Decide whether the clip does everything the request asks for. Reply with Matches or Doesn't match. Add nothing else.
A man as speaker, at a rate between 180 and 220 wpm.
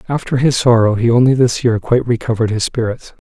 Matches